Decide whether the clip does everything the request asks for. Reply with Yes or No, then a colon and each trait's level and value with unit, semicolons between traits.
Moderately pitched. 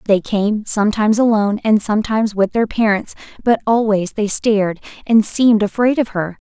No: high, 215 Hz